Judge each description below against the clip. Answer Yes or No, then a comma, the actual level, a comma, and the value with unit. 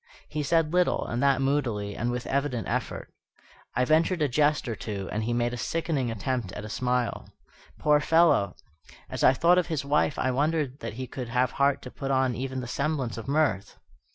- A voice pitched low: Yes, low, 130 Hz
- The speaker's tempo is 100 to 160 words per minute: No, fast, 205 wpm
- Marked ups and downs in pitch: No, average, 3.7 semitones